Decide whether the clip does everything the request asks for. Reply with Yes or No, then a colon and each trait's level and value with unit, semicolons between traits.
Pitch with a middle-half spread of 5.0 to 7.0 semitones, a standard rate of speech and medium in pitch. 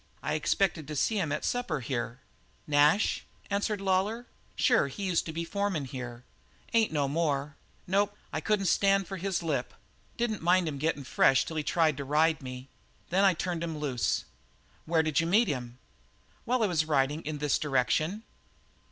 Yes: wide, 5.5 semitones; average, 180 wpm; medium, 160 Hz